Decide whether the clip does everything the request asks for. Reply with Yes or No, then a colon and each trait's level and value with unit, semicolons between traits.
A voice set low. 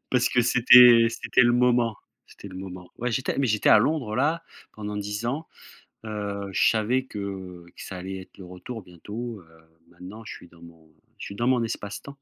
Yes: low, 105 Hz